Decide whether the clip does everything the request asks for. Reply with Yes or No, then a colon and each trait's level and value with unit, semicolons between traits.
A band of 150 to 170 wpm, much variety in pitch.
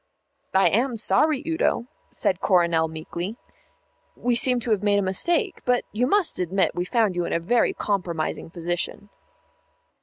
Yes: average, 155 wpm; wide, 5.7 semitones